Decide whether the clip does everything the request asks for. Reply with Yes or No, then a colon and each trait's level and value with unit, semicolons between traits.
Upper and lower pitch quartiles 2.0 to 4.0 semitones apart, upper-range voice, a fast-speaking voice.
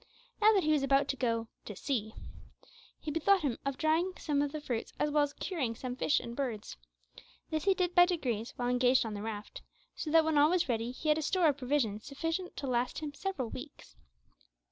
No: average, 4.4 semitones; very high, 285 Hz; fast, 220 wpm